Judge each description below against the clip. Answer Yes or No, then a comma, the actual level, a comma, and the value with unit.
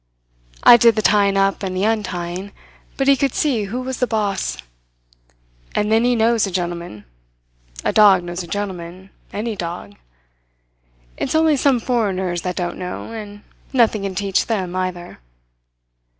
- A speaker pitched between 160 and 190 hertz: No, high, 200 Hz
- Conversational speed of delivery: Yes, average, 155 wpm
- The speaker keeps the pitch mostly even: No, average, 3.9 semitones